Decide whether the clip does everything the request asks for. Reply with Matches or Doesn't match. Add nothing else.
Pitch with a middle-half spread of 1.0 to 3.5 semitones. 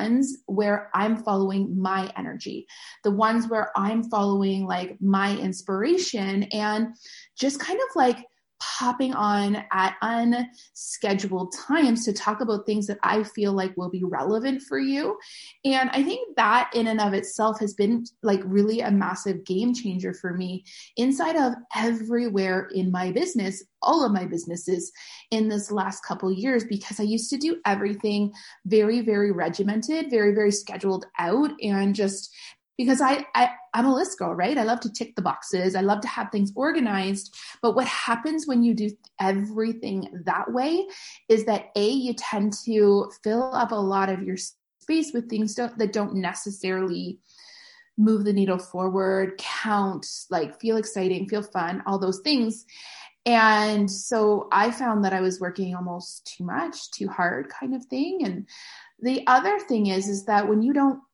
Doesn't match